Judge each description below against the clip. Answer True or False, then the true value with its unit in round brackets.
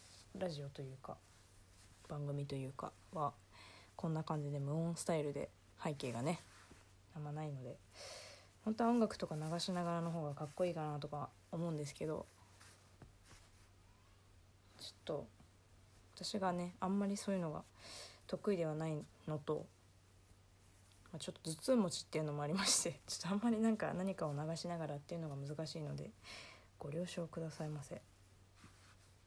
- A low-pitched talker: False (145 Hz)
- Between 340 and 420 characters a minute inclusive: False (320 characters per minute)